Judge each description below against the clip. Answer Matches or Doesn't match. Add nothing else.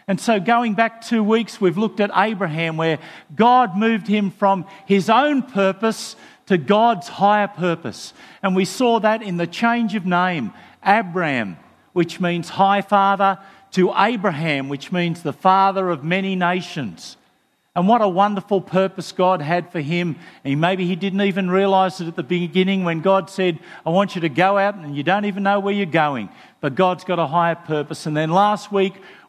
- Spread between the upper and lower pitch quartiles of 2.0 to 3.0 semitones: Matches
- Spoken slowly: Doesn't match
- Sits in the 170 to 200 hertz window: Matches